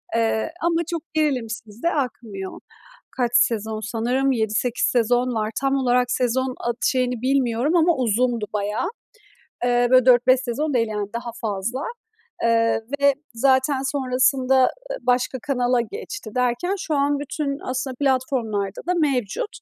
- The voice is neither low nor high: No, very high, 250 Hz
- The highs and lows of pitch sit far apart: No, average, 3.0 semitones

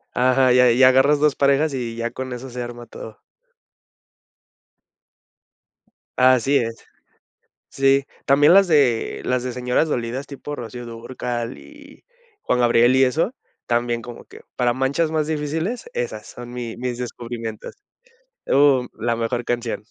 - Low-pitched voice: Yes, low, 125 Hz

